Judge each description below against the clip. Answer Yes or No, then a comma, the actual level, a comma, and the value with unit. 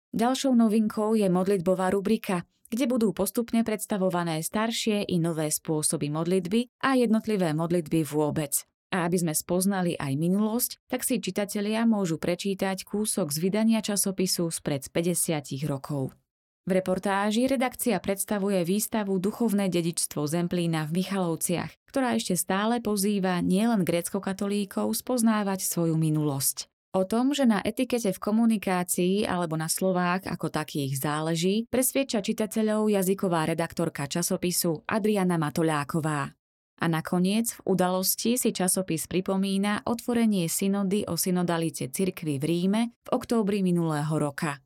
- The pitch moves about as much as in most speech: Yes, average, 4.2 semitones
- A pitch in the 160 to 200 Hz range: Yes, high, 190 Hz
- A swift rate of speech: No, average, 125 wpm